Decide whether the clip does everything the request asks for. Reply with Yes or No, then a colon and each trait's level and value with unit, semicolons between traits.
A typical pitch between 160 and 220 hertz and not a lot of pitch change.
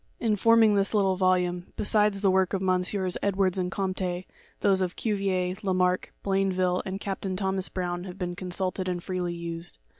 Yes: medium, 185 Hz; narrow, 1.4 semitones